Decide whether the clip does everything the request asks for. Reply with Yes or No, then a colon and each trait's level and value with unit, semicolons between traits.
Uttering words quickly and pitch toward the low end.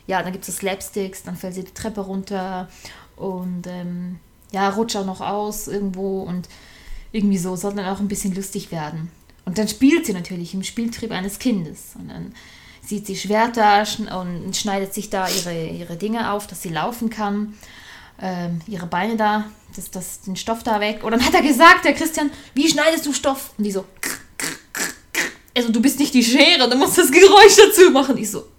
No: fast, 205 wpm; high, 205 Hz